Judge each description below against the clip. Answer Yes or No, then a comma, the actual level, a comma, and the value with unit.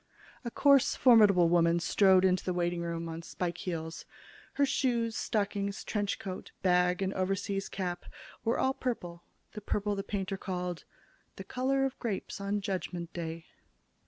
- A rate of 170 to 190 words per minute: No, average, 155 wpm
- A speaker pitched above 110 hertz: Yes, high, 190 Hz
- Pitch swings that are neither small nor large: Yes, average, 3.1 semitones